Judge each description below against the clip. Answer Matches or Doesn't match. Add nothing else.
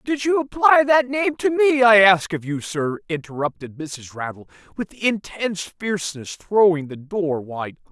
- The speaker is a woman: Doesn't match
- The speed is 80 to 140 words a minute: Doesn't match